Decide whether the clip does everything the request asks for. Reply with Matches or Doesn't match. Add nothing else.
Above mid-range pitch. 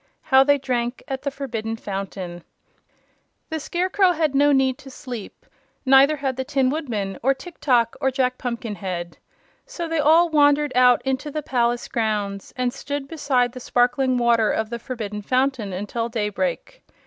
Matches